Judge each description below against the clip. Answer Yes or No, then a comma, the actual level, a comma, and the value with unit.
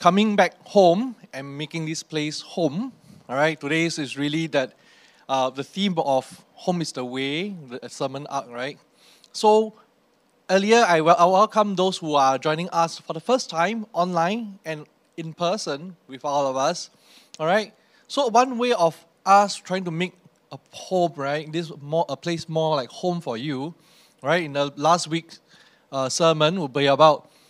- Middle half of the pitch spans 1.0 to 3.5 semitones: No, average, 4.2 semitones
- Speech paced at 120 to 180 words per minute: Yes, average, 175 wpm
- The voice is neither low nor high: Yes, medium, 165 Hz